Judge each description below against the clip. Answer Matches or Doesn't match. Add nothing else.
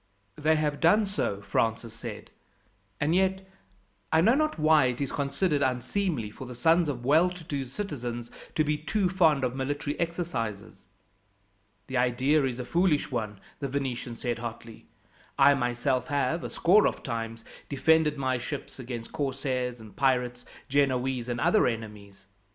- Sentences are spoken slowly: Doesn't match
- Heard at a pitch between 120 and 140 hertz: Matches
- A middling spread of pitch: Matches